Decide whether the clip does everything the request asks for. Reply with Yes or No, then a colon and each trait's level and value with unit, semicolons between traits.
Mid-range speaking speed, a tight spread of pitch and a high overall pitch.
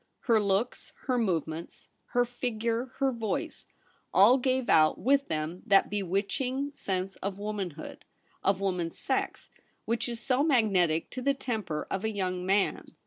No: average, 145 wpm; average, 4.9 semitones; high, 210 Hz